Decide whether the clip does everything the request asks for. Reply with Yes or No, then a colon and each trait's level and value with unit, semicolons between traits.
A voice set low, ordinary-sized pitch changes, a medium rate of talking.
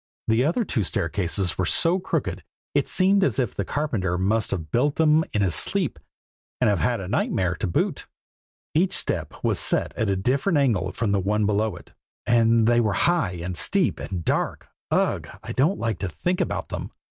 No: low, 110 Hz; wide, 7.4 semitones; average, 195 wpm